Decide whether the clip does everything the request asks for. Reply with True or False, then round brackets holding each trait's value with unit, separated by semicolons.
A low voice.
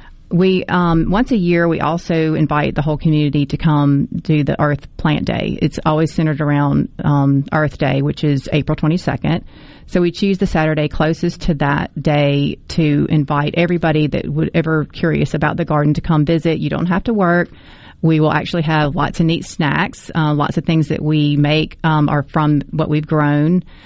False (155 Hz)